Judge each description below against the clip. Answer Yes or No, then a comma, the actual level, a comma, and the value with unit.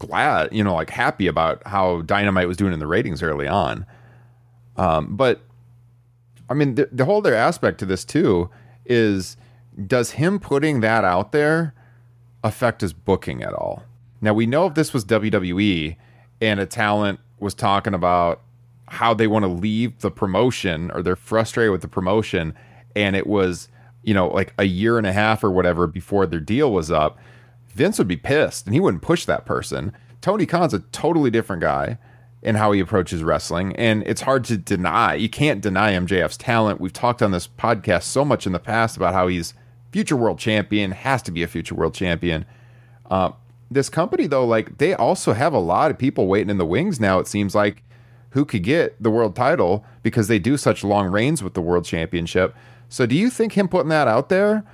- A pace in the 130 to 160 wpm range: No, average, 200 wpm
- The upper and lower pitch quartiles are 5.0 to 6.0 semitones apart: No, average, 4.1 semitones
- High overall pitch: No, low, 110 Hz